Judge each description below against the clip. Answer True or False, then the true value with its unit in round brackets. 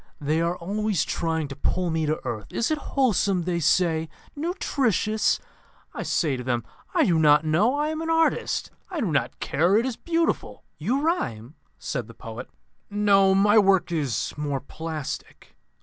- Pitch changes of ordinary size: False (6.3 semitones)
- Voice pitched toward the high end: False (180 Hz)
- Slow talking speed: False (170 wpm)